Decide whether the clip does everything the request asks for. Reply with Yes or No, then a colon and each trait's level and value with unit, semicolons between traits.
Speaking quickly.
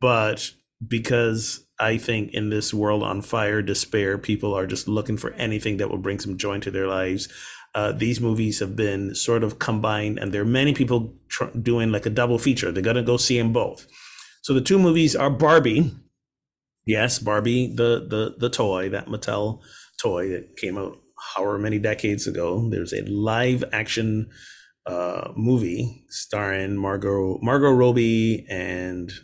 No: average, 170 wpm